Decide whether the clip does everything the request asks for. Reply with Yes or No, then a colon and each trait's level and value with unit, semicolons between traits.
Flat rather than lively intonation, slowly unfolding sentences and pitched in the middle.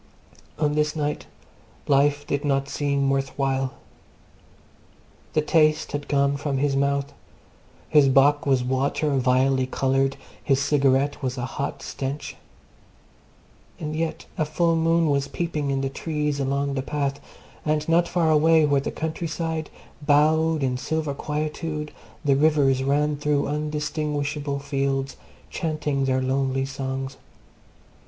Yes: narrow, 1.9 semitones; slow, 130 wpm; medium, 145 Hz